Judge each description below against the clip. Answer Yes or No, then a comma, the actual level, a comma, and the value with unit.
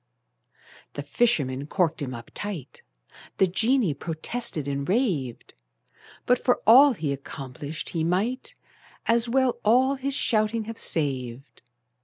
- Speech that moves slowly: Yes, slow, 125 wpm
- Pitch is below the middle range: No, medium, 185 Hz